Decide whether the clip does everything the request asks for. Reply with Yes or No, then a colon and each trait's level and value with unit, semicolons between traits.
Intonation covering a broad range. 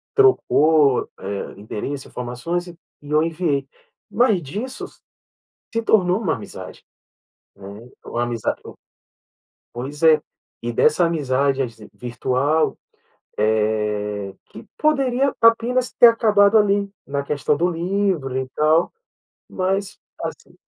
Yes: wide, 8.2 semitones